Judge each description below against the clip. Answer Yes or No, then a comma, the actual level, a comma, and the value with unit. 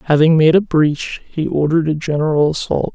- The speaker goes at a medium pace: Yes, average, 185 wpm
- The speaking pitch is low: No, medium, 155 Hz